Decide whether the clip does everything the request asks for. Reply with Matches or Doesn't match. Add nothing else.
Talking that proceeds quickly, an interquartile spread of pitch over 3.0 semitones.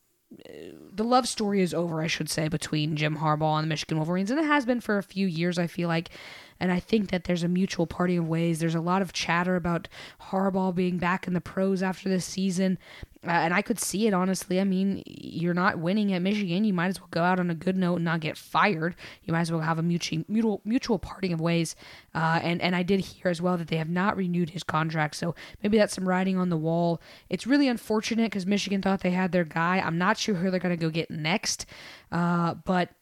Doesn't match